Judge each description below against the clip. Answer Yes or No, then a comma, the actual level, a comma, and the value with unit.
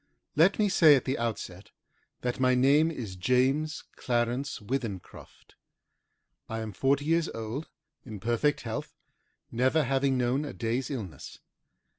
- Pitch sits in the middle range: No, low, 130 Hz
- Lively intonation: No, average, 3.8 semitones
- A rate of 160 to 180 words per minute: No, slow, 135 wpm